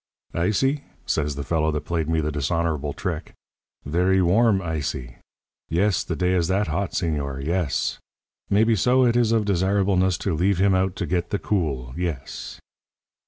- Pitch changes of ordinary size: Yes, average, 4.2 semitones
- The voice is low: Yes, very low, 90 Hz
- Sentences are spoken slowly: No, average, 165 wpm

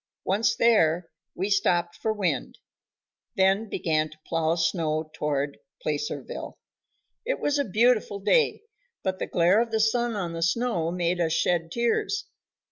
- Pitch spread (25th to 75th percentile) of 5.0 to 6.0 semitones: Yes, average, 5.3 semitones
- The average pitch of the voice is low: No, medium, 185 Hz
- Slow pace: No, average, 145 wpm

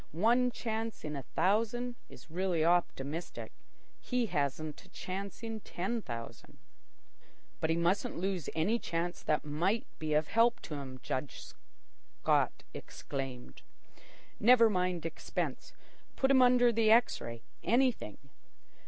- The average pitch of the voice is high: No, medium, 180 Hz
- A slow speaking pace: Yes, slow, 125 wpm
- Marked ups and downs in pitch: Yes, wide, 6.9 semitones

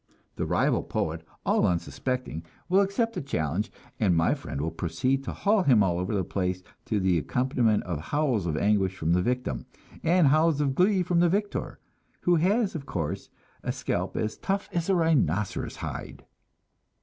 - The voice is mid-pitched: No, low, 125 Hz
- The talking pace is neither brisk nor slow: Yes, average, 175 wpm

